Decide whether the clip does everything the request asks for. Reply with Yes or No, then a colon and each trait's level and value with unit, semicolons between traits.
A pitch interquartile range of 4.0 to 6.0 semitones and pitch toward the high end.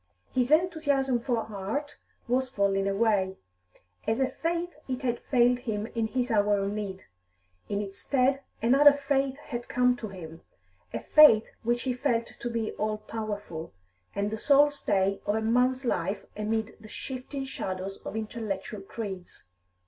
Yes: average, 4.4 semitones; high, 230 Hz